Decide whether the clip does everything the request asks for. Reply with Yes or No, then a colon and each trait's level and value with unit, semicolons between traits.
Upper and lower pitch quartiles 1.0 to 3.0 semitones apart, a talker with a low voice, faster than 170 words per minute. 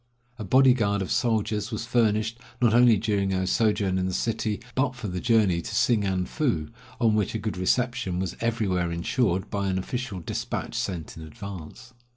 No: average, 3.9 semitones; low, 105 Hz; average, 185 wpm